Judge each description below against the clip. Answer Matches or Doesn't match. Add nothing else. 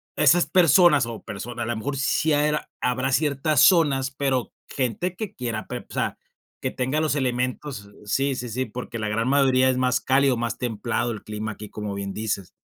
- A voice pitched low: Matches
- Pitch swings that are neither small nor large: Matches